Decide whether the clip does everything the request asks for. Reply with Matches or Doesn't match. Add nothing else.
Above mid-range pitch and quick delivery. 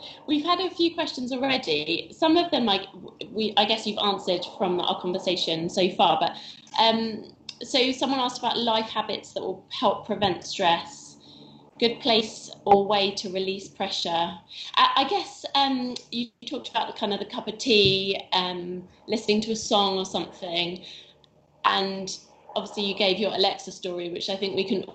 Doesn't match